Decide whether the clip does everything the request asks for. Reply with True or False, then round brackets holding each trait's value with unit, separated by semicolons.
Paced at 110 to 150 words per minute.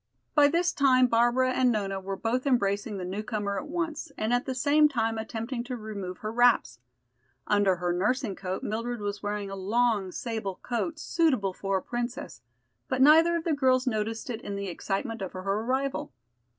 False (185 wpm)